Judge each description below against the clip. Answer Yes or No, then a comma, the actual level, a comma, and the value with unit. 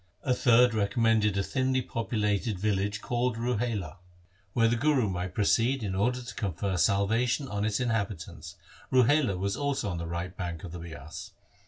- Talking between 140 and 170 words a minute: Yes, average, 165 wpm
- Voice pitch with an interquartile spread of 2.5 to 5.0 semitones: Yes, average, 4.4 semitones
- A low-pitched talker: Yes, low, 105 Hz